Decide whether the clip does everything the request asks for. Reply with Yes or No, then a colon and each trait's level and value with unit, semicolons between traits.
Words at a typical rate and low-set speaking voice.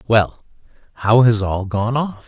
Yes: average, 160 wpm; low, 110 Hz